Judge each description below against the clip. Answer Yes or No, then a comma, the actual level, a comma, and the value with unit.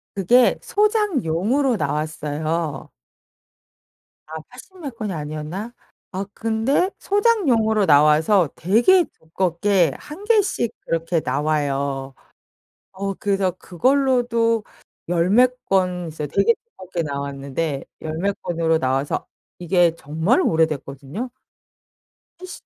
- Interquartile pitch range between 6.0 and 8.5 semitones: Yes, wide, 7.4 semitones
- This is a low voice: No, medium, 185 Hz